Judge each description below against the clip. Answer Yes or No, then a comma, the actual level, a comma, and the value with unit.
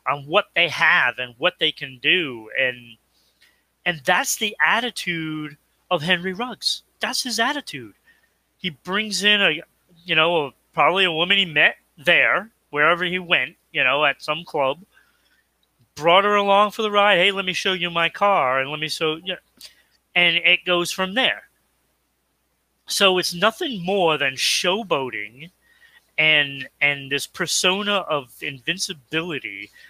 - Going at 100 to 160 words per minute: Yes, average, 155 wpm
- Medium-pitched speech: Yes, medium, 175 Hz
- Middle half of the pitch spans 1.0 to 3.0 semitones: No, average, 4.6 semitones